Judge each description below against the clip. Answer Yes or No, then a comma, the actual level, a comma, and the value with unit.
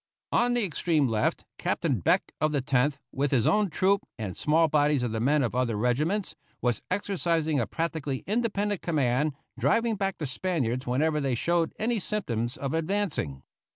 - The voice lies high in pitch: No, medium, 150 Hz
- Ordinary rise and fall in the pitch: No, wide, 6.8 semitones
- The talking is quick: No, average, 170 wpm